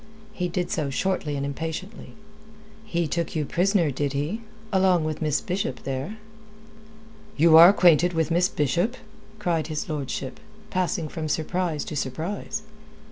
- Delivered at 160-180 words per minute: No, average, 140 wpm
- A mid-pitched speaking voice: Yes, medium, 165 Hz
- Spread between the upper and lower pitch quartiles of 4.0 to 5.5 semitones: No, average, 3.5 semitones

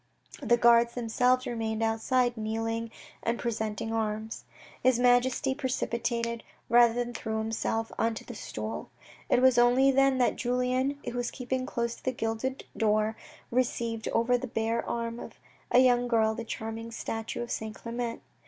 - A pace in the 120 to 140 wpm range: No, average, 160 wpm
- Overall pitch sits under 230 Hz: No, high, 235 Hz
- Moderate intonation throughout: No, narrow, 1.7 semitones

